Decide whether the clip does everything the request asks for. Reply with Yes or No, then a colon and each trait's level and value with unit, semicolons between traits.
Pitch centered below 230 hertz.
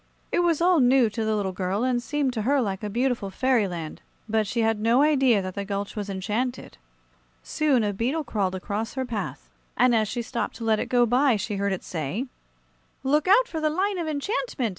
No: high, 235 Hz